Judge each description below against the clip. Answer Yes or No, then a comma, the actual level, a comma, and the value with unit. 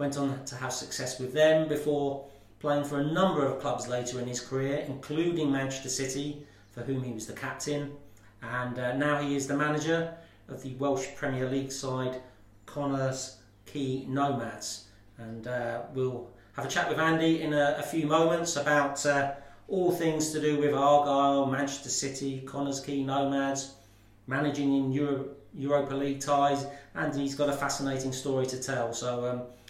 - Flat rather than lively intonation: Yes, narrow, 2.1 semitones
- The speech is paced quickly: No, average, 170 wpm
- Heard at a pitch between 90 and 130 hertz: No, medium, 140 Hz